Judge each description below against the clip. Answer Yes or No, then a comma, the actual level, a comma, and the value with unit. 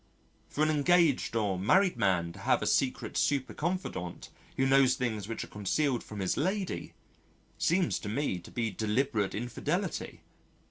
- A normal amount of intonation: No, wide, 6.6 semitones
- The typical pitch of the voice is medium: No, low, 125 Hz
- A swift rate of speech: No, average, 155 wpm